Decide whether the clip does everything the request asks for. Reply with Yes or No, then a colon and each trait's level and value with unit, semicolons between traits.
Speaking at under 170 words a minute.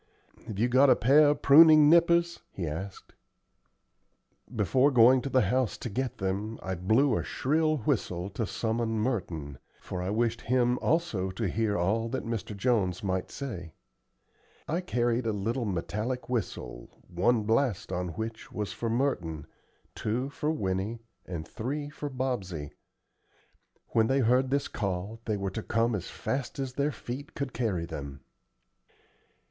Yes: average, 155 wpm